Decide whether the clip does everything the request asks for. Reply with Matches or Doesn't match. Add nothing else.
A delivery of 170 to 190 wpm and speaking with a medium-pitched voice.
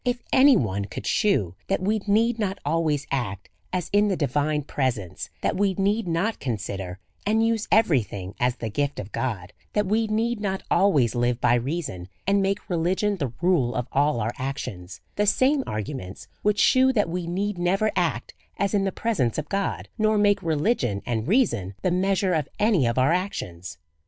Matches